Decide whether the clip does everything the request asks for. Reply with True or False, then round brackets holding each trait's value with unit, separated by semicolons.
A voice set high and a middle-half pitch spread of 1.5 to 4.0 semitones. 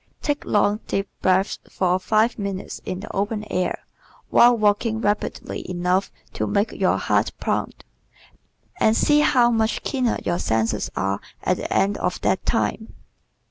True (205 Hz; 3.4 semitones)